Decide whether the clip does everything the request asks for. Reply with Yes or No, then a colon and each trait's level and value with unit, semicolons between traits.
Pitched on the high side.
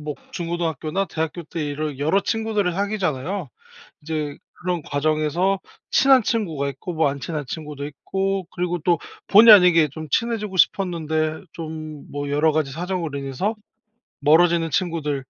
No: medium, 160 Hz